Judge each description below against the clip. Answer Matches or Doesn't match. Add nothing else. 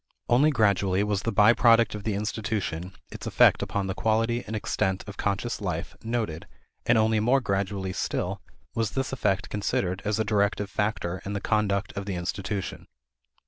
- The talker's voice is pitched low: Matches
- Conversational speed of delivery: Matches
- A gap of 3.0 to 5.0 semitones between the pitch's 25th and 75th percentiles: Doesn't match